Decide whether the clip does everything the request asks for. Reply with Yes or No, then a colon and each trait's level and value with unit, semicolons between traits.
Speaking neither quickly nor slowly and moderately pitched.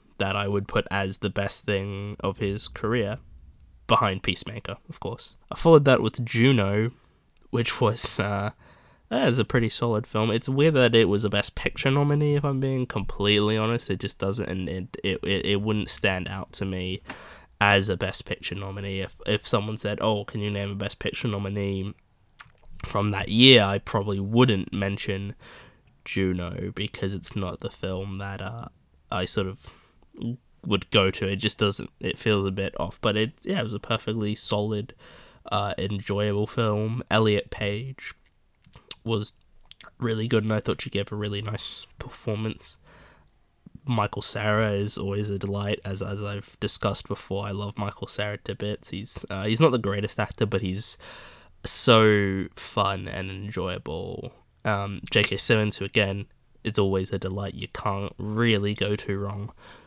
No: average, 170 wpm; low, 105 Hz